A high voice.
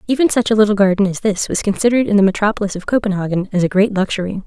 Yes: high, 205 Hz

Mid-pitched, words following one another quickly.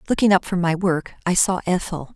Yes: medium, 180 Hz; fast, 225 wpm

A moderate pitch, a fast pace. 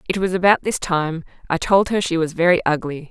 Yes: medium, 175 Hz; fast, 230 wpm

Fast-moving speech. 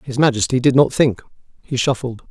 No: average, 180 wpm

